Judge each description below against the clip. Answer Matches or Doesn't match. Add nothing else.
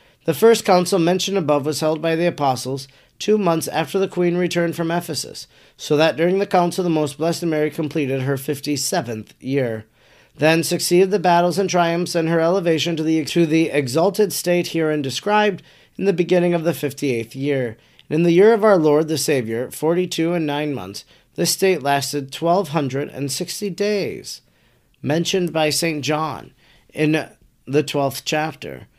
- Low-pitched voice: Doesn't match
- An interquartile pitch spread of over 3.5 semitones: Doesn't match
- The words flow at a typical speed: Matches